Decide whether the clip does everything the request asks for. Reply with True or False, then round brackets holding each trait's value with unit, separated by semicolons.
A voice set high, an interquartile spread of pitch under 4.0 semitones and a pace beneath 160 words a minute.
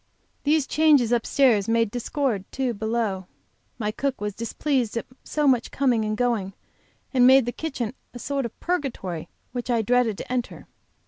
False (245 Hz; 3.5 semitones; 170 wpm)